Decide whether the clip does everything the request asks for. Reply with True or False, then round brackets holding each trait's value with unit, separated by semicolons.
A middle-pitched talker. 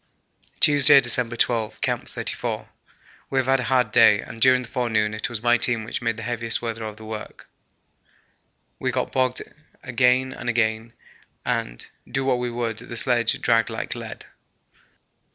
False (120 Hz)